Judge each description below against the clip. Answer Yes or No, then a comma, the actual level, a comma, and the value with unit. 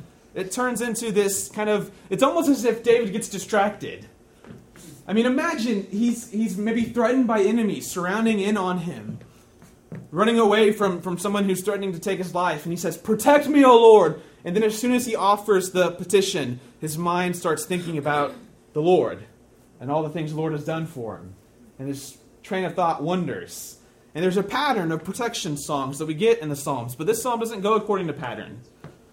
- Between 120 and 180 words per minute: No, average, 200 wpm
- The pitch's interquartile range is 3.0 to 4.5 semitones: No, wide, 5.6 semitones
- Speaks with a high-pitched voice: Yes, high, 195 Hz